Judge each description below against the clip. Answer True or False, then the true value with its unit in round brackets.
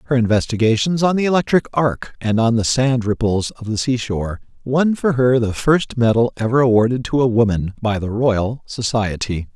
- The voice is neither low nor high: False (120 Hz)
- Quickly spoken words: False (180 wpm)